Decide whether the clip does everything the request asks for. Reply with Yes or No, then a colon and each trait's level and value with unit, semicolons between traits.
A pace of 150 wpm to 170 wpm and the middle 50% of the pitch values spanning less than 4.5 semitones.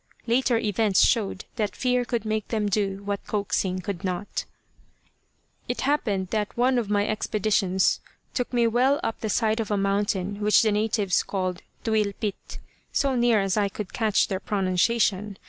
Yes: average, 165 wpm; narrow, 2.5 semitones